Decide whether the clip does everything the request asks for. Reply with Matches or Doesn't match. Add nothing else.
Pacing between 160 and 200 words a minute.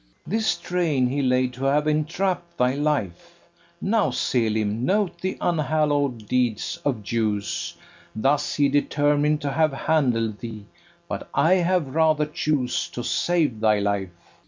Doesn't match